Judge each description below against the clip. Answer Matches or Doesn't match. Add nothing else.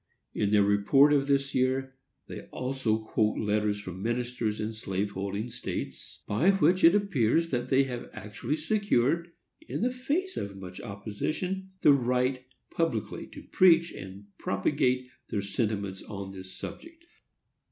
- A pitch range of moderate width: Doesn't match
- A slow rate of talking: Doesn't match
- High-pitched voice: Doesn't match